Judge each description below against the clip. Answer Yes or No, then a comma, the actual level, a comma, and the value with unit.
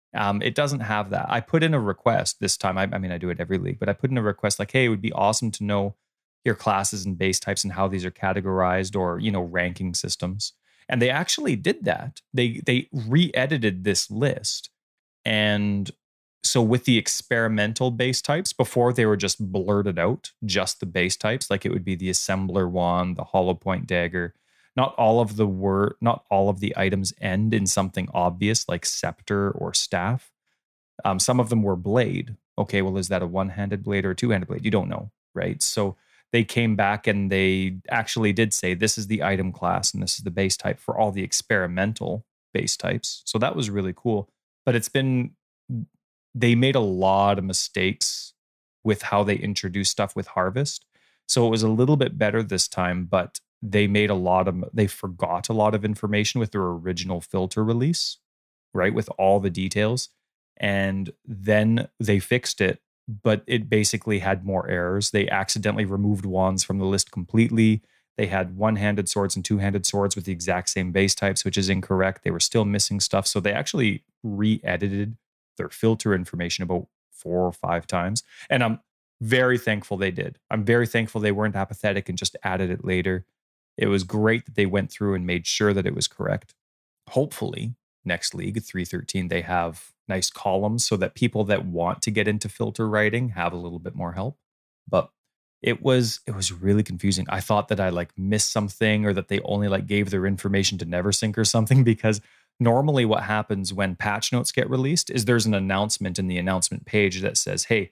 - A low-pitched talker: Yes, low, 100 Hz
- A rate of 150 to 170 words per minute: No, average, 200 wpm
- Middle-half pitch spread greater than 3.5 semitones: No, average, 2.7 semitones